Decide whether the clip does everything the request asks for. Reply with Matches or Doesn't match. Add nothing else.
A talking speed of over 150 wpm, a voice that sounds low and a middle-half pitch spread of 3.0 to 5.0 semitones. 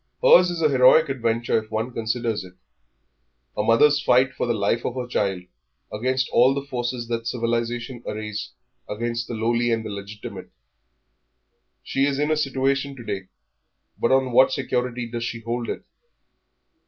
Doesn't match